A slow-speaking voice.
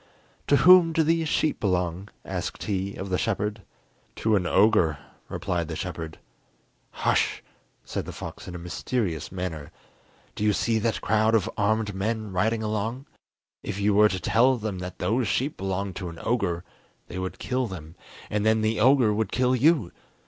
No: average, 175 wpm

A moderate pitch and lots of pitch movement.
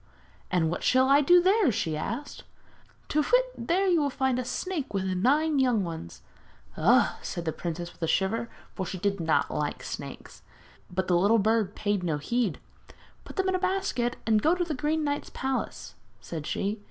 No: high, 235 Hz; wide, 8.3 semitones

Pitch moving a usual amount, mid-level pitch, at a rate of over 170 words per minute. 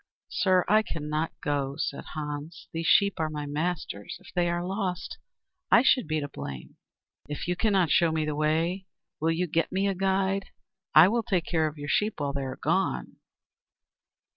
Yes: average, 4.0 semitones; medium, 165 Hz; average, 185 wpm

